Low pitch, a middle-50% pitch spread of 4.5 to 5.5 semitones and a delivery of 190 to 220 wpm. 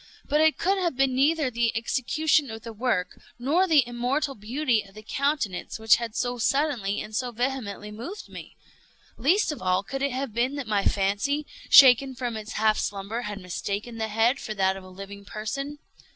No: high, 240 Hz; average, 4.8 semitones; average, 195 wpm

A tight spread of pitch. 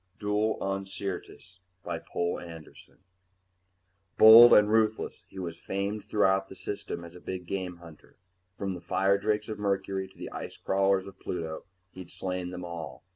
Yes: narrow, 2.3 semitones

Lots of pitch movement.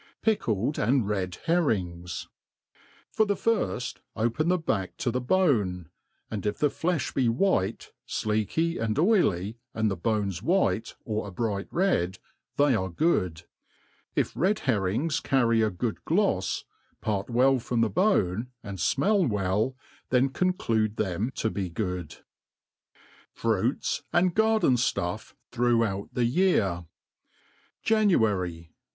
Yes: wide, 8.0 semitones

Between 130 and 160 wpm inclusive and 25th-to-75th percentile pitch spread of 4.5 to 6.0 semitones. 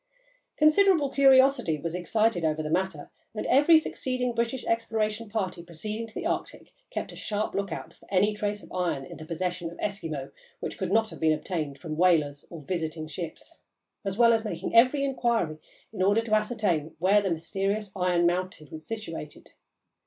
No: average, 175 wpm; wide, 5.5 semitones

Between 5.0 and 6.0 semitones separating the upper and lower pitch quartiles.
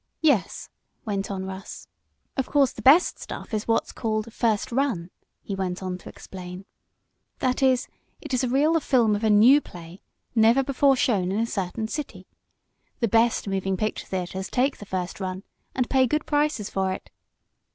Yes: wide, 5.4 semitones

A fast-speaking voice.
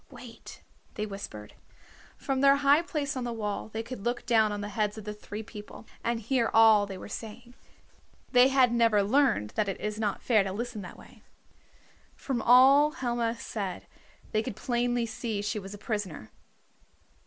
No: average, 180 wpm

